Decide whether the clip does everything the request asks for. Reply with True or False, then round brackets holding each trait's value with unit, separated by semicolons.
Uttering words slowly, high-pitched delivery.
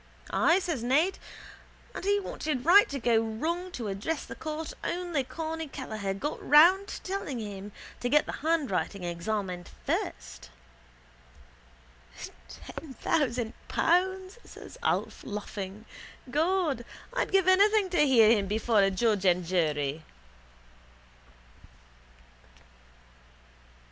True (115 wpm; 260 Hz)